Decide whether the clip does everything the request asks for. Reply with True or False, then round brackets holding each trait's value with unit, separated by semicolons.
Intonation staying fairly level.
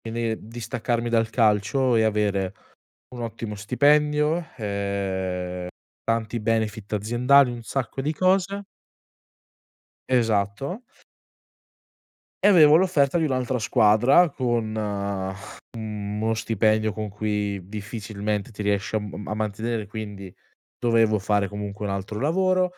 False (3.6 semitones)